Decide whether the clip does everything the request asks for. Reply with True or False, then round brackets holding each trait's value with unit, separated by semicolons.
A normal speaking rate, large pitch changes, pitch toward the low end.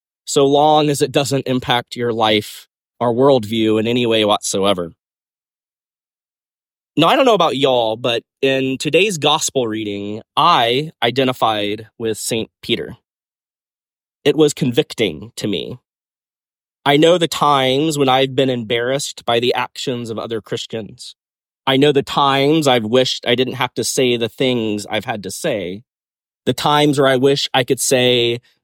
False (155 wpm; 3.4 semitones; 130 Hz)